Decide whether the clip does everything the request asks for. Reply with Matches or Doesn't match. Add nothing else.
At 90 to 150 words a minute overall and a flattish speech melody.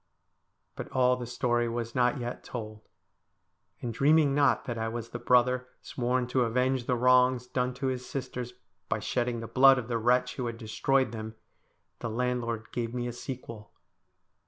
Doesn't match